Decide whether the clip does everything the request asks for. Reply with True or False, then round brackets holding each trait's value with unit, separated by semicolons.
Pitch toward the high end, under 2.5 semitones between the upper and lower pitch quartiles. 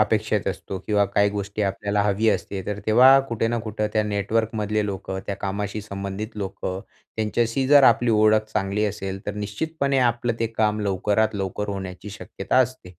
False (105 Hz; 2.0 semitones)